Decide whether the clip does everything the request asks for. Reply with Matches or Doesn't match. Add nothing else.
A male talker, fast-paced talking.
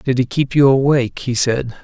Matches